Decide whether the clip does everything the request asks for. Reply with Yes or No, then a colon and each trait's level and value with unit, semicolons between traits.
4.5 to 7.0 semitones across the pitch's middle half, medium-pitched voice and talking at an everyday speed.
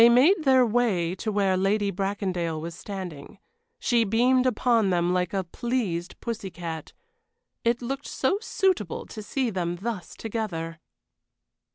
No: average, 5.2 semitones; high, 205 Hz; average, 145 wpm